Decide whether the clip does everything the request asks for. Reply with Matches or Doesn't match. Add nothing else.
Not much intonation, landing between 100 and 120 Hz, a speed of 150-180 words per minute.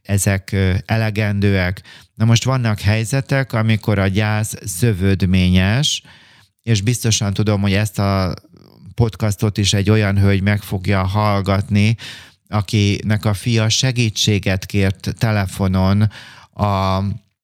Doesn't match